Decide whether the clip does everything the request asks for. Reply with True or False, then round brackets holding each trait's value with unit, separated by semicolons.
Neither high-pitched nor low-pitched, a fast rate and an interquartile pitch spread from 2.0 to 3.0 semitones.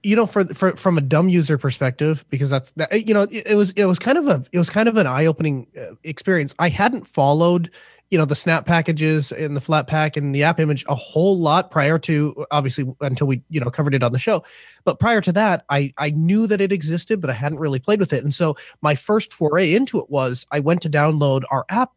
False (155 Hz; 250 wpm; 4.7 semitones)